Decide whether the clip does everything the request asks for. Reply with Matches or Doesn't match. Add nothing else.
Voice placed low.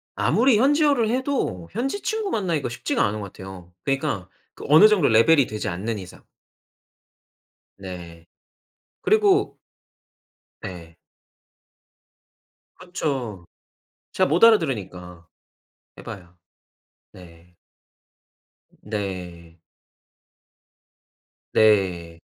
Matches